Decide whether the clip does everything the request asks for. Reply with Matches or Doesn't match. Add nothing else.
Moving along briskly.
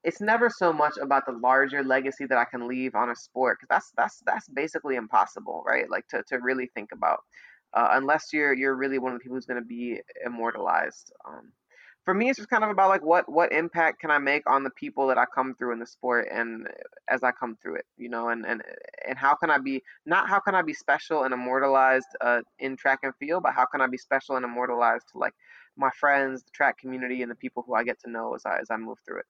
Matches